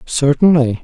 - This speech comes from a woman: No, male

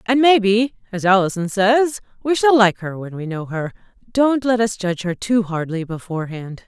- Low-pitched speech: No, high, 205 Hz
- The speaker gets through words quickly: No, average, 190 wpm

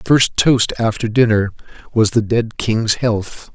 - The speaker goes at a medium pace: Yes, average, 170 wpm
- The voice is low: Yes, low, 110 Hz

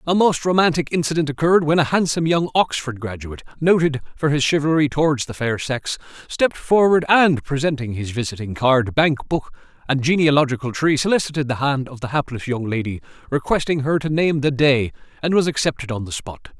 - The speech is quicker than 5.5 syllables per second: Yes, 5.8 syllables/s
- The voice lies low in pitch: No, medium, 145 Hz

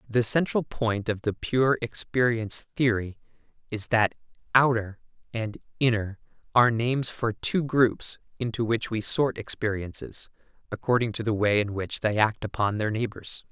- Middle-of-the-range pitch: No, low, 115 Hz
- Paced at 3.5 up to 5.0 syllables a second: Yes, 4.7 syllables/s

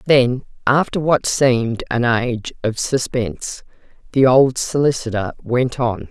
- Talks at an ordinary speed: No, slow, 130 wpm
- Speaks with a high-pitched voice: No, low, 125 Hz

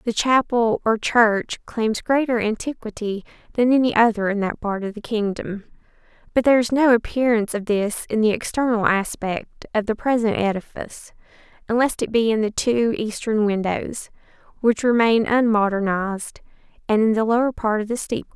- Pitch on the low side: No, high, 220 Hz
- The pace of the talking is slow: No, average, 165 wpm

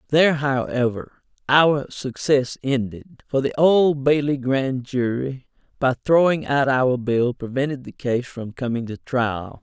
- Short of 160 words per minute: Yes, average, 145 wpm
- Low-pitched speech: Yes, low, 130 Hz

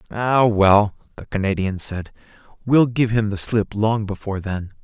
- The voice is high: No, low, 105 Hz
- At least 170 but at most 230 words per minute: No, average, 160 wpm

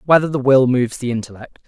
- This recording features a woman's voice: No, male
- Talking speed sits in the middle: No, fast, 215 wpm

